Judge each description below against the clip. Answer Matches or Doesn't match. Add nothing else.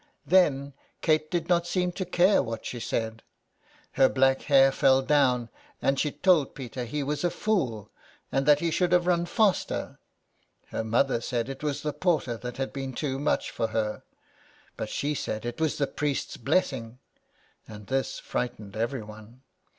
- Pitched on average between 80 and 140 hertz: Matches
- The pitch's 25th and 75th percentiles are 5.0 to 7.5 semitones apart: Doesn't match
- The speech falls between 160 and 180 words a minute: Matches